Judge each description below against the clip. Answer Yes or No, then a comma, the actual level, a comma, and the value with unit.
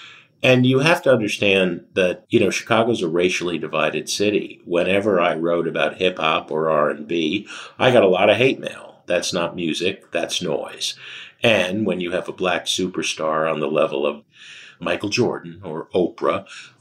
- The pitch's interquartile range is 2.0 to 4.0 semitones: No, average, 4.5 semitones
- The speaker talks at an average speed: Yes, average, 170 wpm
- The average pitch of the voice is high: No, very low, 90 Hz